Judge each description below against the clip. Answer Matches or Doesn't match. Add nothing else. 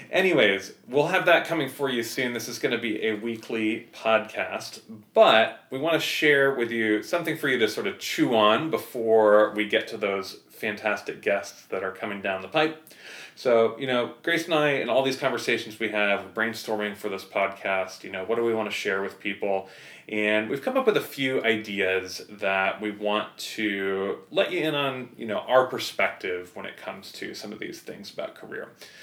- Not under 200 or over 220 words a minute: Matches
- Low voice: Matches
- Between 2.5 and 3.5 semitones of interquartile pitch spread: Doesn't match